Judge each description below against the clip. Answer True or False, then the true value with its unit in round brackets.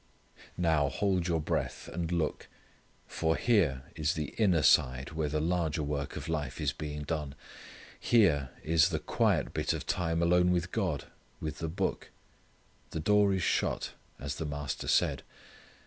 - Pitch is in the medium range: False (80 Hz)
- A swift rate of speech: False (160 wpm)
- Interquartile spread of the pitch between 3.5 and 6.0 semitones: False (3.0 semitones)